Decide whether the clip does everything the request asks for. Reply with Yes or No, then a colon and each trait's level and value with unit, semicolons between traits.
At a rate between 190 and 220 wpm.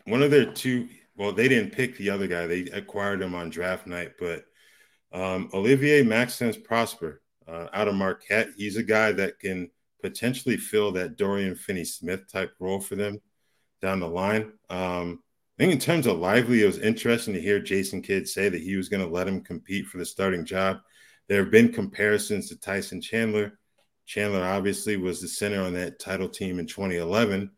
Yes: average, 195 wpm